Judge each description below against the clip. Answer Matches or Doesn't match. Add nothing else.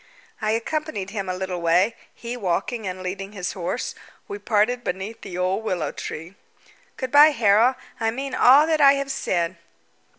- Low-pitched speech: Doesn't match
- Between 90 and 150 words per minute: Doesn't match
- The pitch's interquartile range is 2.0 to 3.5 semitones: Doesn't match